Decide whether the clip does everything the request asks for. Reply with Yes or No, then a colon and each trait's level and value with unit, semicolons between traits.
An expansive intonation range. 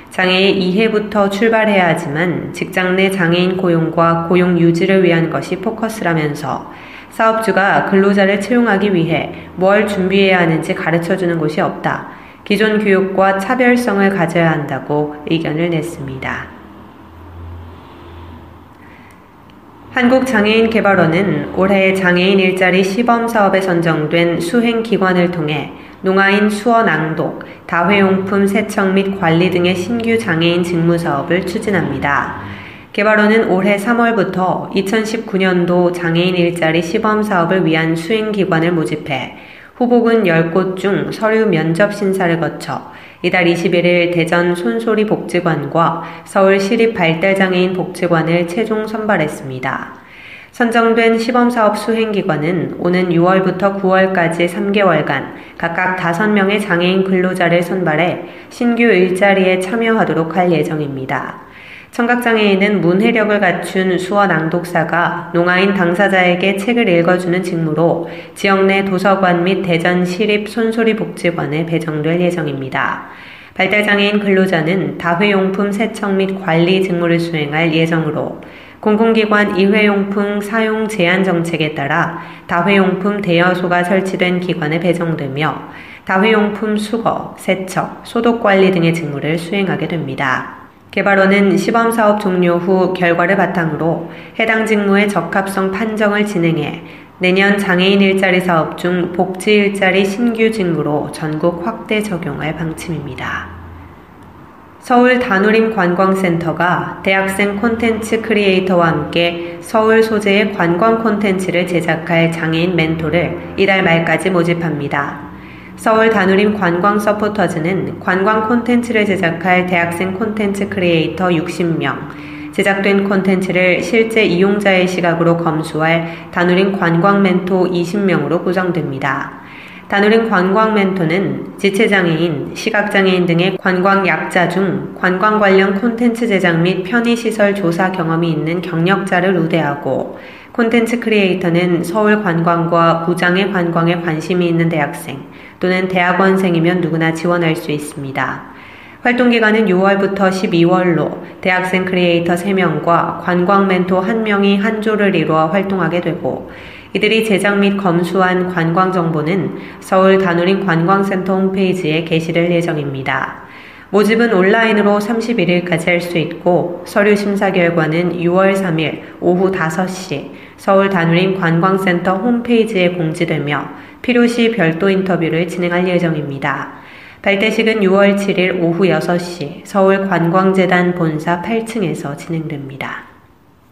No: average, 3.1 semitones